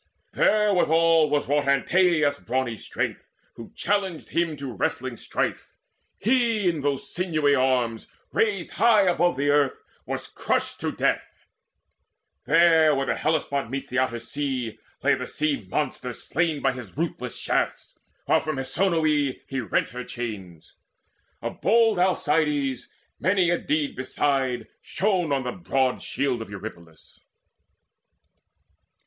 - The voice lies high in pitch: No, medium, 145 Hz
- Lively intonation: No, average, 4.8 semitones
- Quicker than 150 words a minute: No, slow, 135 wpm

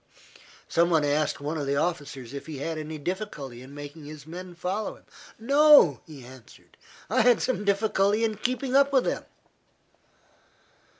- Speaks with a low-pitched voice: No, medium, 165 Hz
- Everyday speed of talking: Yes, average, 165 wpm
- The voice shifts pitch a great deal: Yes, wide, 6.8 semitones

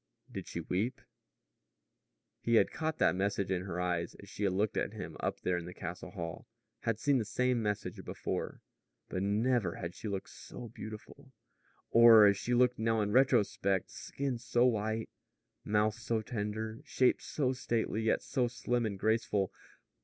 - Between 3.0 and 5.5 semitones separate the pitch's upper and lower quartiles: Yes, average, 3.4 semitones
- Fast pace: No, average, 170 wpm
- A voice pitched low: Yes, low, 110 Hz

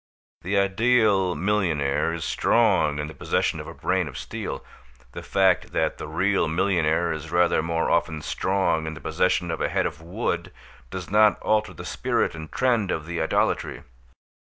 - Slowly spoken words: No, average, 175 wpm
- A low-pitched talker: Yes, very low, 85 Hz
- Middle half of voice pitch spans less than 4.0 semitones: Yes, average, 3.4 semitones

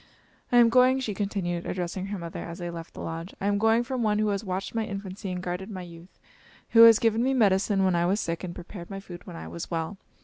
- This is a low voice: No, high, 195 Hz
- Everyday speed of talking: No, fast, 260 wpm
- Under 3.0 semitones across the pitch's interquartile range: No, average, 3.8 semitones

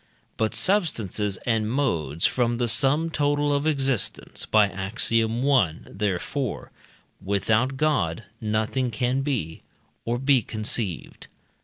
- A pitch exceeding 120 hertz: No, low, 115 Hz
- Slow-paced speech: Yes, slow, 115 wpm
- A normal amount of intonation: Yes, average, 4.6 semitones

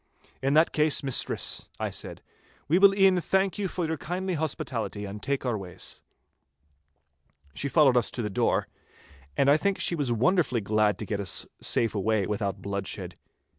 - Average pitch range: No, wide, 8.0 semitones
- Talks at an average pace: Yes, average, 170 wpm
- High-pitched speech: No, low, 135 Hz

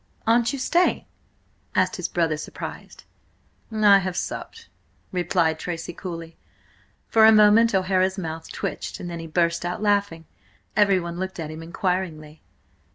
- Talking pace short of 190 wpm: Yes, average, 140 wpm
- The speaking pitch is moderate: Yes, medium, 180 Hz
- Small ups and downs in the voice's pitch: No, average, 3.8 semitones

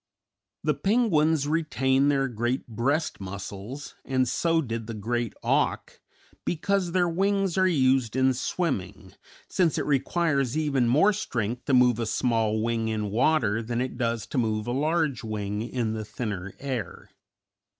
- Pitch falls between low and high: No, low, 130 Hz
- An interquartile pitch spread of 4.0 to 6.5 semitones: Yes, wide, 5.5 semitones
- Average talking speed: Yes, average, 150 wpm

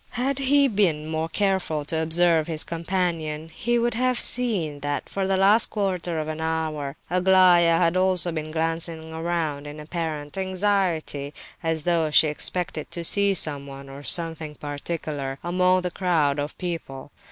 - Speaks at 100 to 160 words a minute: Yes, average, 155 wpm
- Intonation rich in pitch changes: No, average, 3.3 semitones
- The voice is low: No, medium, 165 Hz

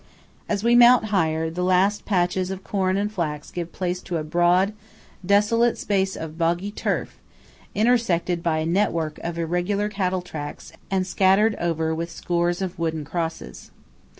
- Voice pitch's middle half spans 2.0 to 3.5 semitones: Yes, average, 3.1 semitones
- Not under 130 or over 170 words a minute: Yes, average, 155 wpm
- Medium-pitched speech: Yes, medium, 180 Hz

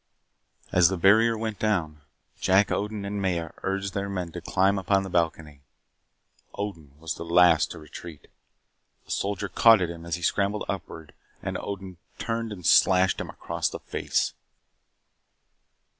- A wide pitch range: No, average, 3.1 semitones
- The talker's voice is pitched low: Yes, very low, 95 Hz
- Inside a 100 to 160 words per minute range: Yes, average, 155 wpm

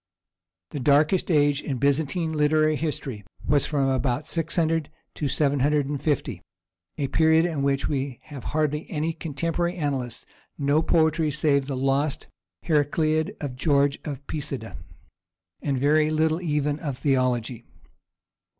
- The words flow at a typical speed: No, slow, 125 wpm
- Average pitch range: No, narrow, 2.3 semitones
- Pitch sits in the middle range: Yes, medium, 145 Hz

